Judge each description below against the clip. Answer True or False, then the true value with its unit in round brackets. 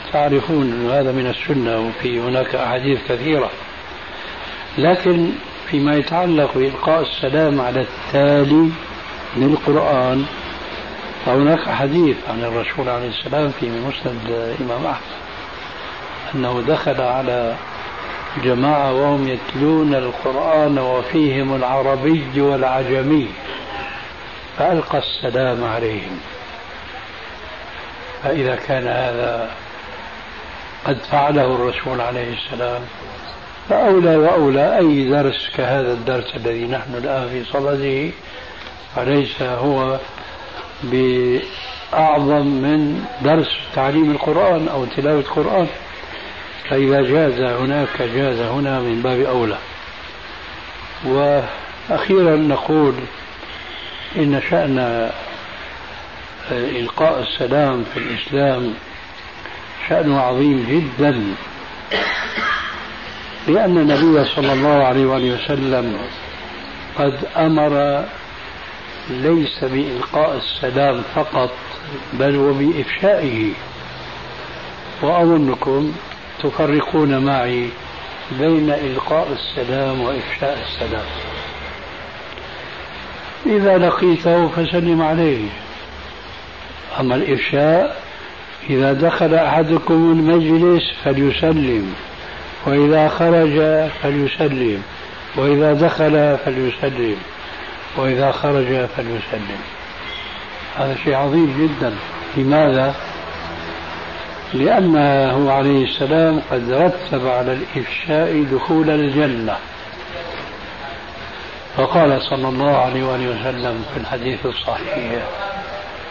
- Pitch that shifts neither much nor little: True (3.3 semitones)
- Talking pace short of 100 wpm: True (80 wpm)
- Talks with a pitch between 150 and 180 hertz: False (135 Hz)